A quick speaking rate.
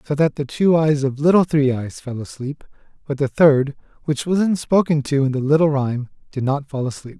Yes: fast, 225 wpm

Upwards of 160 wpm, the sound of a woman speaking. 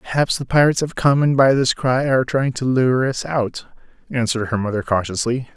No: fast, 205 wpm; male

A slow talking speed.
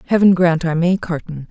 No: average, 200 wpm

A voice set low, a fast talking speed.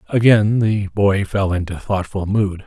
No: low, 100 Hz; average, 180 wpm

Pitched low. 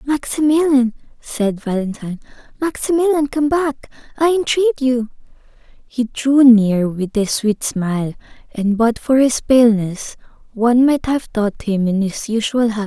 No: high, 245 Hz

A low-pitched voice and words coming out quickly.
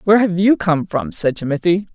No: medium, 180 Hz; fast, 215 wpm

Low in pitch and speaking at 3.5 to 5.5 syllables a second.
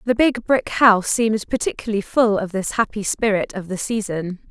No: high, 210 Hz; 5.4 syllables/s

